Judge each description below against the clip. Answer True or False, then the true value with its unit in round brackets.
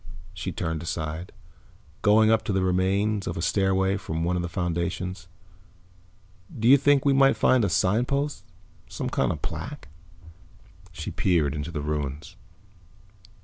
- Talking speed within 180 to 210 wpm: False (145 wpm)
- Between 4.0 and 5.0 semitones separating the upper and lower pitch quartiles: True (4.3 semitones)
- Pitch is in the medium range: False (95 Hz)